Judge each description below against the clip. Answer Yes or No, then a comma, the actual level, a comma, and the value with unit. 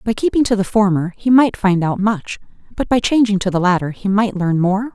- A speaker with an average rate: No, fast, 240 wpm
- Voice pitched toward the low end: No, high, 205 Hz